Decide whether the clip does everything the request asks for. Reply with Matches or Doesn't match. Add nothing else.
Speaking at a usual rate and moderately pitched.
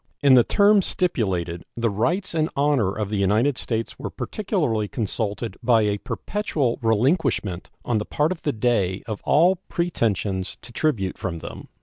Doesn't match